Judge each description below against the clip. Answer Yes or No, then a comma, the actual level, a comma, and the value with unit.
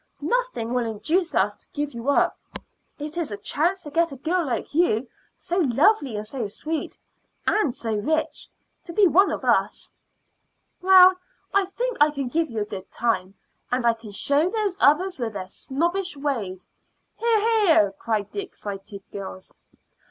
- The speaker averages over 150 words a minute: Yes, average, 175 wpm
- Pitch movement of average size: No, wide, 8.3 semitones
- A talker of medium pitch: No, very high, 290 Hz